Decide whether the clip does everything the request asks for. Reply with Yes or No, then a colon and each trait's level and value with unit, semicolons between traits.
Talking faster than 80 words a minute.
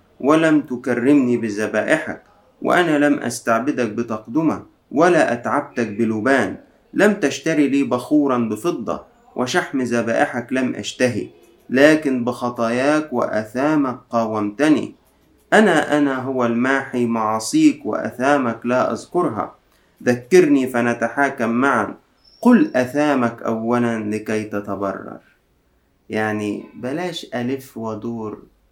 Yes: average, 90 wpm